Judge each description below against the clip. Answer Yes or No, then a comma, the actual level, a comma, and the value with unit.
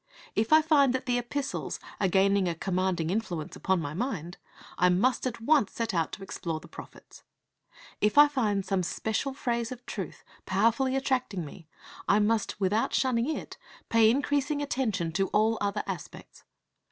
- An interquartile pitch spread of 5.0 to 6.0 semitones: Yes, wide, 5.5 semitones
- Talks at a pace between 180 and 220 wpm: No, average, 165 wpm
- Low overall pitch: No, high, 220 Hz